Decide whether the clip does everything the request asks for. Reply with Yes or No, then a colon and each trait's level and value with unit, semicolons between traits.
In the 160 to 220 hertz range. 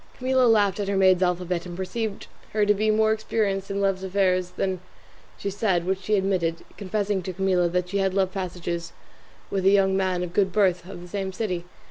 Yes: high, 190 Hz